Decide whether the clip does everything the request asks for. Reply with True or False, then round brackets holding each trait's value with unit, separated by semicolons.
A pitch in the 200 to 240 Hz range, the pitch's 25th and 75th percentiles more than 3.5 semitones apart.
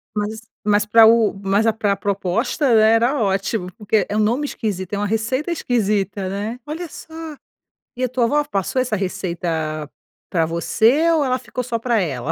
True (215 Hz; 4.0 semitones)